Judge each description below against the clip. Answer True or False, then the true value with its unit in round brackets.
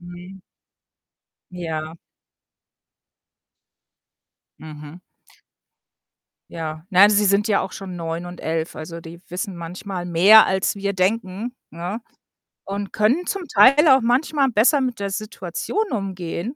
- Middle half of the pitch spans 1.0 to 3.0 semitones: False (4.2 semitones)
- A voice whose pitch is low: False (190 Hz)